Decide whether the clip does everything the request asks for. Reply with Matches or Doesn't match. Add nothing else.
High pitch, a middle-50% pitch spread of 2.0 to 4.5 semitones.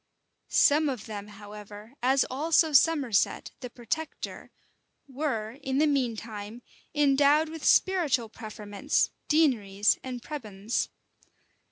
Doesn't match